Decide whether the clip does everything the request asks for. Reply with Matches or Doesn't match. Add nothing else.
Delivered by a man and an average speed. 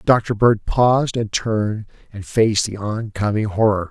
Matches